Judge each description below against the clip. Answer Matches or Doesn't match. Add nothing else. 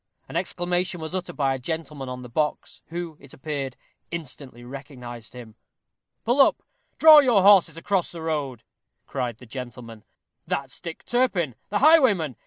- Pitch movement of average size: Doesn't match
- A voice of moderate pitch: Matches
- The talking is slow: Doesn't match